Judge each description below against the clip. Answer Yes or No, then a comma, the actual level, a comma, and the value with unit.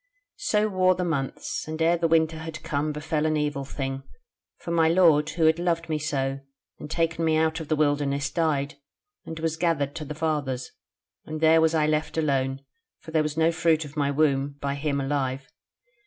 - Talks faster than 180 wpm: Yes, average, 200 wpm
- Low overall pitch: No, medium, 155 Hz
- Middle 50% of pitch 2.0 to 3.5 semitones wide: Yes, narrow, 2.4 semitones